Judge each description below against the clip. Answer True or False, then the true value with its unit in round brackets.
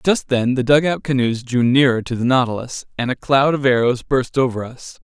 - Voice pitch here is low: True (130 Hz)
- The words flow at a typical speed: False (215 wpm)